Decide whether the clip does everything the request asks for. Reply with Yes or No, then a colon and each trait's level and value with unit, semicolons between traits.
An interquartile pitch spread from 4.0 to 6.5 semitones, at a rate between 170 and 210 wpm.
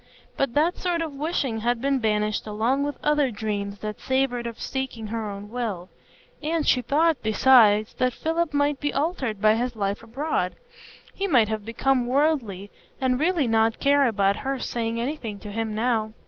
Yes: average, 4.8 semitones; average, 175 wpm